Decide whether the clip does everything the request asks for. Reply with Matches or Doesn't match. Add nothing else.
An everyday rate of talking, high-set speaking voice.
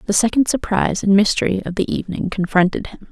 Matches